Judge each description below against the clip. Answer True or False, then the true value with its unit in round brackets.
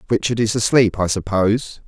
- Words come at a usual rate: True (160 wpm)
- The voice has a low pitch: True (105 Hz)